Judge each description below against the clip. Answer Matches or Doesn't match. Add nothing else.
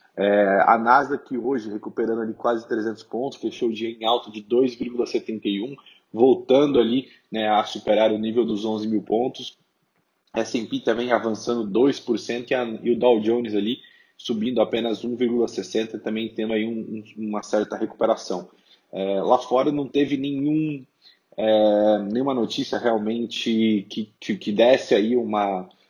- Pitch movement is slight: Matches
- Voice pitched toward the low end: Matches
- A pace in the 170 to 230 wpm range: Doesn't match